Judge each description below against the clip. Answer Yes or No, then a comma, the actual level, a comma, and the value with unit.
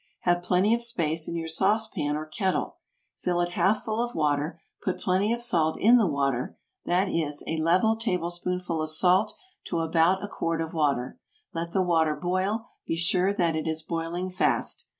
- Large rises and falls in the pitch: No, average, 3.0 semitones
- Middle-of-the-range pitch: Yes, medium, 175 Hz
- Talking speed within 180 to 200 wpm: Yes, average, 190 wpm